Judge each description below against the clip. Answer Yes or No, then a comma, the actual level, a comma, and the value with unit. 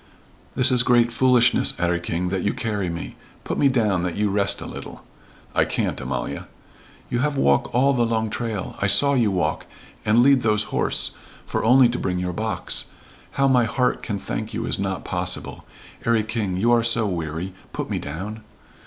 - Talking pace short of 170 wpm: No, average, 190 wpm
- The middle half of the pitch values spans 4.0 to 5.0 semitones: Yes, average, 4.7 semitones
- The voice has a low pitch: Yes, low, 110 Hz